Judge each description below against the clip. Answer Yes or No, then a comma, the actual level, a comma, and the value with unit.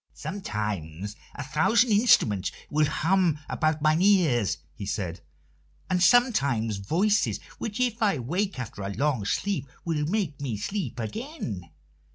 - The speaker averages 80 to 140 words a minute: Yes, slow, 135 wpm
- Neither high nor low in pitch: Yes, medium, 150 Hz